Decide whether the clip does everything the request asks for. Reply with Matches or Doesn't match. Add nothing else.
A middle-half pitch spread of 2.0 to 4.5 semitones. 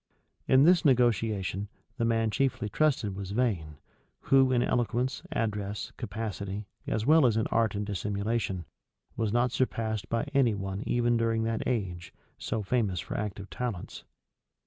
Matches